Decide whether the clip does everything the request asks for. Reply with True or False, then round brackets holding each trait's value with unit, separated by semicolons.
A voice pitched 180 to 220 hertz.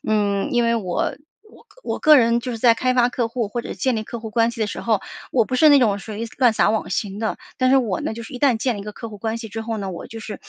False (230 Hz)